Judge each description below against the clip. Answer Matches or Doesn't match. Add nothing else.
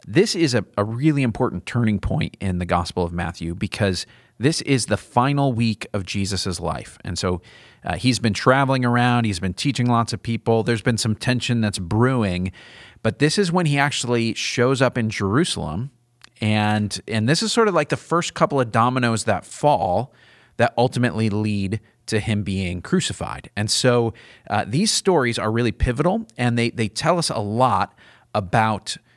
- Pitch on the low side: Matches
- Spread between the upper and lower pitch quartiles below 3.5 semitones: Doesn't match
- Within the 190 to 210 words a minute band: Doesn't match